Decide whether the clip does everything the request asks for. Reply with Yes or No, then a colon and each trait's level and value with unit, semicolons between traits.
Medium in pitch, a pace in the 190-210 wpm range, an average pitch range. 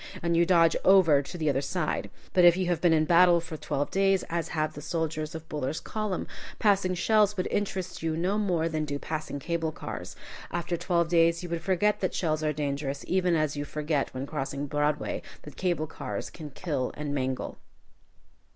Yes: medium, 165 Hz; average, 195 wpm; average, 3.1 semitones